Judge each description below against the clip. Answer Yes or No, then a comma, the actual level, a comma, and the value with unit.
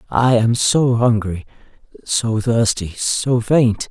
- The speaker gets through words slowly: Yes, slow, 125 wpm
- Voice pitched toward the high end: No, low, 115 Hz